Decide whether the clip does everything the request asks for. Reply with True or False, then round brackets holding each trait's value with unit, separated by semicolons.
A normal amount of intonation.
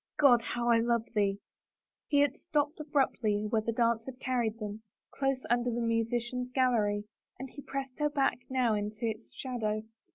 True (3.1 semitones)